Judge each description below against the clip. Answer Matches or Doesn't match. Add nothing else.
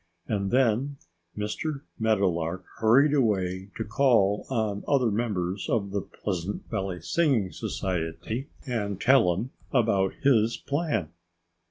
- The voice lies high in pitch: Doesn't match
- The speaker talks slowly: Matches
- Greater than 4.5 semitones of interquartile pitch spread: Matches